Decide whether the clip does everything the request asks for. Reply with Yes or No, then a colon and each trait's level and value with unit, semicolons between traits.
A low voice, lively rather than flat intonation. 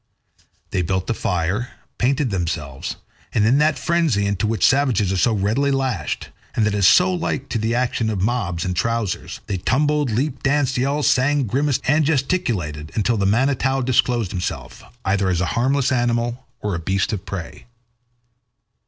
Yes: low, 115 Hz; wide, 5.7 semitones